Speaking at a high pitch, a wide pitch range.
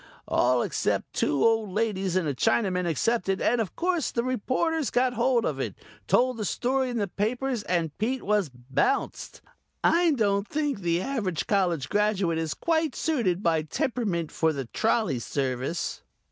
Yes: high, 210 Hz; wide, 6.8 semitones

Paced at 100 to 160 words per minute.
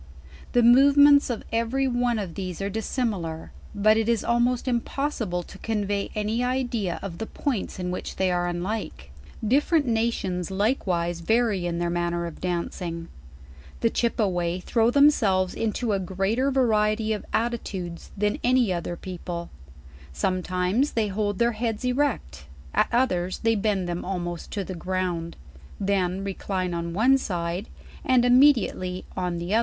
Yes: average, 155 wpm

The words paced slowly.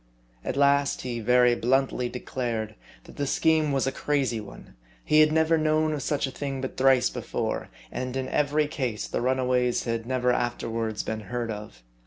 No: average, 185 wpm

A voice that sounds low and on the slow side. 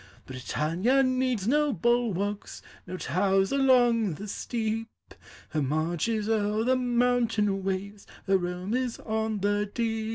No: high, 215 Hz; slow, 130 wpm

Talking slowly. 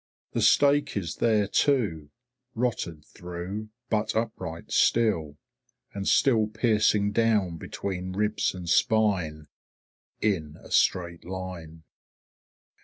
Yes: slow, 105 wpm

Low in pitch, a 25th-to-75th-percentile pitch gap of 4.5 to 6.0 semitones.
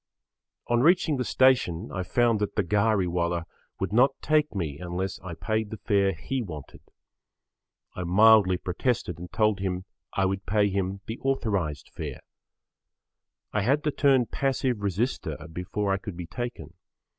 Yes: low, 100 Hz; average, 5.0 semitones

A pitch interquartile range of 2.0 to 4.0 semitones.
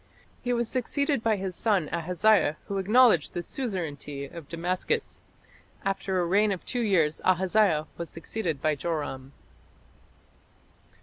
No: average, 5.1 semitones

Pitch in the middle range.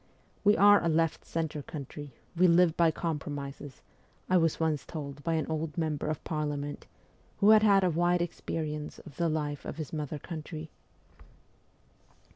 Yes: medium, 160 Hz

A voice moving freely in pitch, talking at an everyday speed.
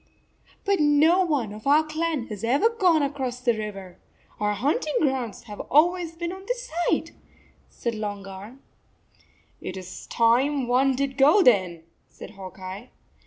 Yes: wide, 6.7 semitones; average, 165 wpm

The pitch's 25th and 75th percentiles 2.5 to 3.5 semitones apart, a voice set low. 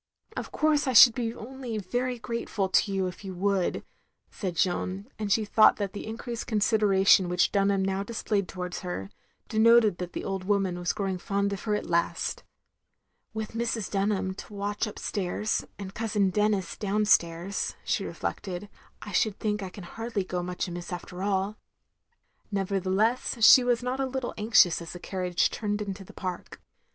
No: average, 2.8 semitones; high, 200 Hz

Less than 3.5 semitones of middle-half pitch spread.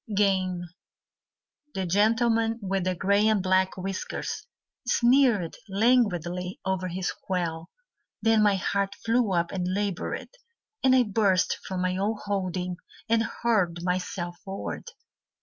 Yes: average, 3.1 semitones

